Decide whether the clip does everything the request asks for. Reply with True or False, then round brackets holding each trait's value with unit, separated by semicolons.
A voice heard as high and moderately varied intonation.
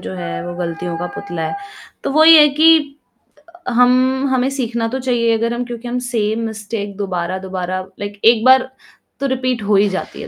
True (225 Hz; 4.9 semitones)